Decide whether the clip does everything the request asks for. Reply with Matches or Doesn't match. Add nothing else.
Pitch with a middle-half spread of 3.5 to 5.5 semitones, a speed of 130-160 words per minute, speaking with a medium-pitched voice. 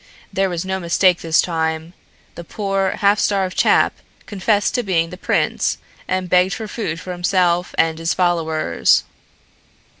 Doesn't match